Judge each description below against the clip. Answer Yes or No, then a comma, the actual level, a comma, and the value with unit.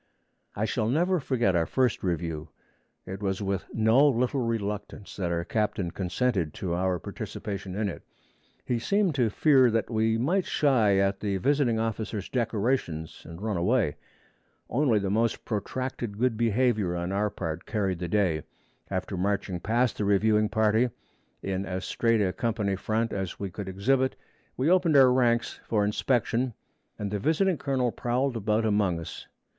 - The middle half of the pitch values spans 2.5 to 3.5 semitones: No, average, 4.2 semitones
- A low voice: Yes, low, 110 Hz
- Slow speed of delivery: No, average, 160 wpm